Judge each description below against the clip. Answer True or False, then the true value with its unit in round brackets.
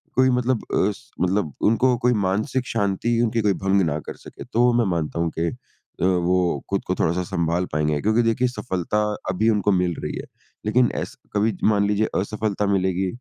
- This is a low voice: True (100 Hz)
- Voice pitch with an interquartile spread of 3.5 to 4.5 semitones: True (4.0 semitones)